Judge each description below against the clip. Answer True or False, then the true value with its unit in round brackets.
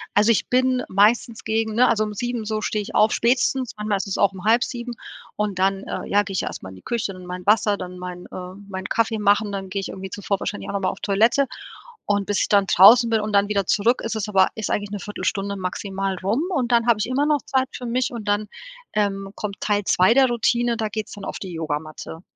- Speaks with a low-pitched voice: False (210 Hz)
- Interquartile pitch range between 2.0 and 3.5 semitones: True (2.9 semitones)